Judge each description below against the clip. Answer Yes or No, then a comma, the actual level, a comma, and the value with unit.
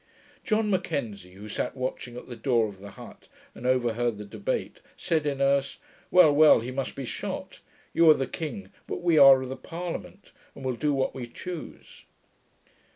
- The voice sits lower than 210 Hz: Yes, low, 135 Hz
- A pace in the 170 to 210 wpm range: Yes, average, 180 wpm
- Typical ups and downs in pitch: Yes, average, 4.6 semitones